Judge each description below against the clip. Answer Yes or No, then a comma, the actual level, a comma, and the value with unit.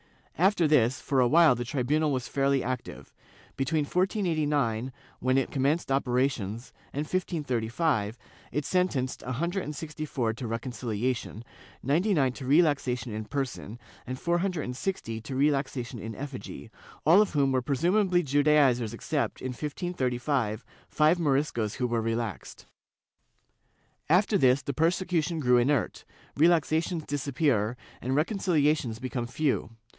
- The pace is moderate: No, slow, 130 wpm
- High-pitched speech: No, medium, 140 Hz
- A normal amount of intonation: Yes, average, 4.2 semitones